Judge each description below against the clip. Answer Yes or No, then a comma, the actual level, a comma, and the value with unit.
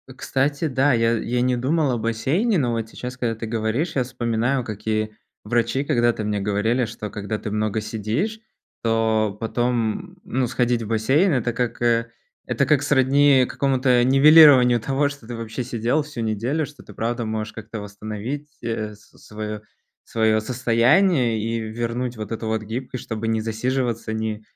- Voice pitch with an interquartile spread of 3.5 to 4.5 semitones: No, average, 3.1 semitones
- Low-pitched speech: Yes, low, 115 Hz